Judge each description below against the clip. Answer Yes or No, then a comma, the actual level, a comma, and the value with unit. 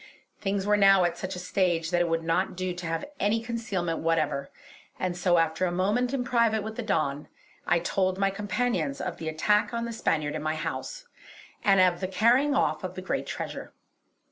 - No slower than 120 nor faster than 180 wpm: No, average, 200 wpm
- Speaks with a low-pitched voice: No, medium, 185 Hz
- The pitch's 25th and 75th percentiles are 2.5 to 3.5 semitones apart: No, average, 4.6 semitones